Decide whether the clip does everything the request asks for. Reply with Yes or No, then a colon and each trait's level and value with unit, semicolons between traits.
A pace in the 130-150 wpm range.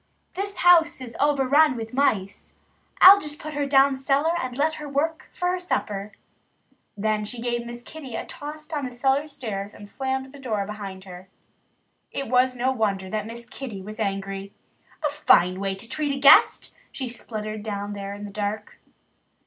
No: average, 185 wpm